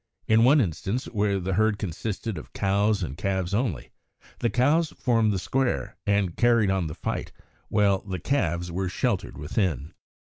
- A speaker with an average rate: Yes, average, 160 wpm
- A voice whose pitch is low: Yes, low, 100 Hz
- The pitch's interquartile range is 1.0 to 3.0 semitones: No, average, 4.0 semitones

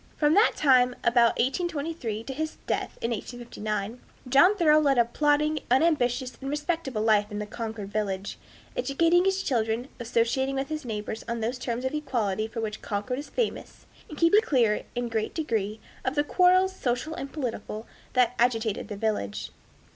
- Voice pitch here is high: Yes, very high, 250 Hz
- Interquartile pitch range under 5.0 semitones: No, average, 5.3 semitones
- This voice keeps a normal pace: Yes, average, 170 wpm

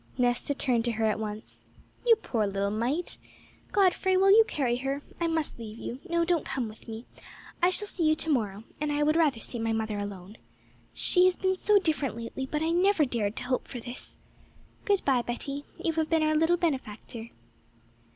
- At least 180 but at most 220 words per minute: Yes, average, 200 wpm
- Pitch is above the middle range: Yes, very high, 275 Hz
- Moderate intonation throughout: No, wide, 6.7 semitones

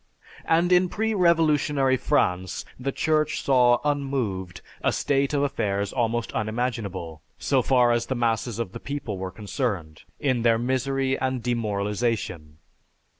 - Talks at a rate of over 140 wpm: No, slow, 135 wpm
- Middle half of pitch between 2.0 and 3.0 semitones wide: No, average, 4.9 semitones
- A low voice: Yes, low, 120 Hz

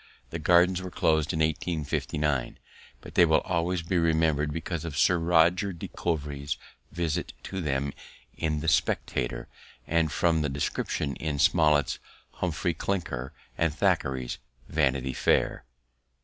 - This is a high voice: No, very low, 80 Hz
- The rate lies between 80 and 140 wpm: Yes, slow, 135 wpm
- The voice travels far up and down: No, narrow, 2.6 semitones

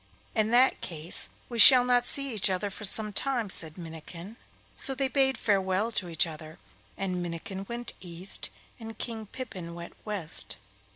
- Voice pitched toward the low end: No, high, 200 Hz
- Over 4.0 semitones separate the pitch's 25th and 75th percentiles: Yes, wide, 5.4 semitones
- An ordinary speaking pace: Yes, average, 165 wpm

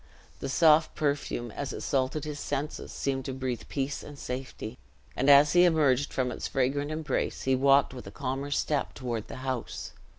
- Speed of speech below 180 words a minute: No, average, 185 wpm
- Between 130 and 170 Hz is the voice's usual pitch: Yes, low, 135 Hz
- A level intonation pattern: Yes, narrow, 2.0 semitones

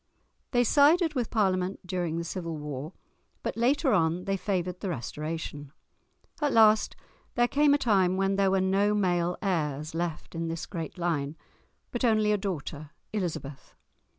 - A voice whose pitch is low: No, medium, 185 Hz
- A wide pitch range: No, average, 4.4 semitones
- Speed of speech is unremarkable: Yes, average, 155 wpm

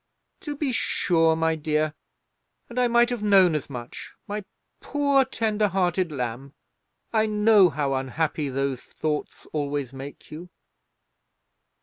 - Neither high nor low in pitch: Yes, medium, 165 Hz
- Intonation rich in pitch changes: Yes, wide, 6.9 semitones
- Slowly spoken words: Yes, slow, 130 wpm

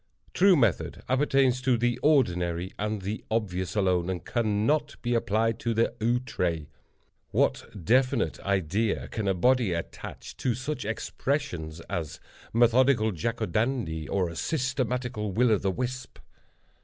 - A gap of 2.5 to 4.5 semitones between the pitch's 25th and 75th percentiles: No, average, 5.3 semitones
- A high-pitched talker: No, low, 115 Hz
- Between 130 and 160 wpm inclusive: Yes, average, 140 wpm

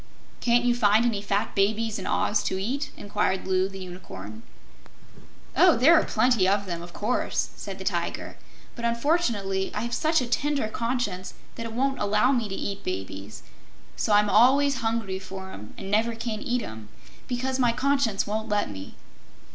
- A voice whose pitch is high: Yes, high, 215 Hz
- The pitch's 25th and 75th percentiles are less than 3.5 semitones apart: No, average, 4.2 semitones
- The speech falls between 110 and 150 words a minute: No, average, 175 wpm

